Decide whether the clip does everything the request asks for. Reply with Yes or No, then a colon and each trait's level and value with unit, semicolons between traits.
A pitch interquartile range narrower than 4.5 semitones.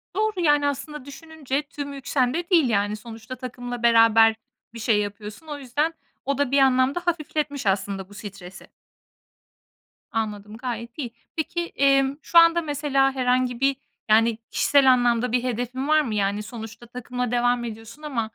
Yes: average, 4.1 semitones